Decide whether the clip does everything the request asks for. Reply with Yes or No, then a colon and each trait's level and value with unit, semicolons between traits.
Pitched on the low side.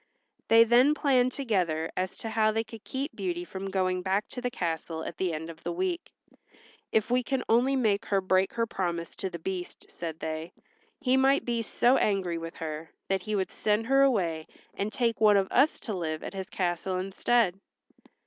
No: high, 200 Hz